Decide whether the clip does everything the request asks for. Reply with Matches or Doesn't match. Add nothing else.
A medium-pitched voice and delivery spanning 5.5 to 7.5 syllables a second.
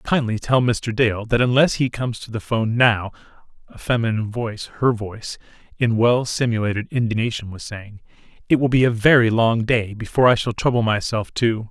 Doesn't match